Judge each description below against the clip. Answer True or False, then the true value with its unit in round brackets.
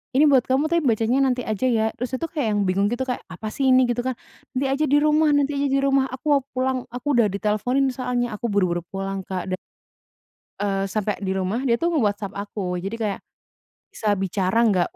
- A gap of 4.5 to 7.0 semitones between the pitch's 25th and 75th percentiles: True (4.9 semitones)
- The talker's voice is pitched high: True (235 Hz)